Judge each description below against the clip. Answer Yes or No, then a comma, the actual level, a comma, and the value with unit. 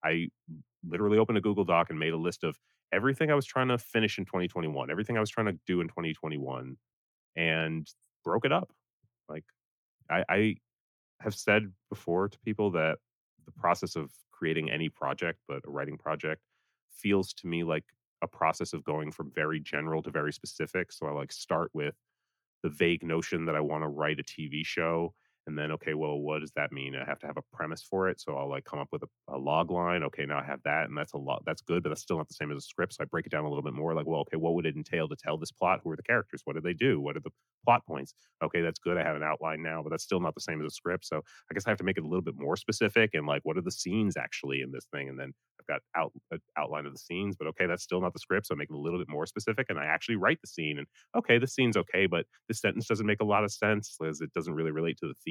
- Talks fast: Yes, fast, 275 wpm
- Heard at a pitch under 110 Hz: Yes, very low, 80 Hz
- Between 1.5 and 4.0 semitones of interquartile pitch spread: No, average, 5.0 semitones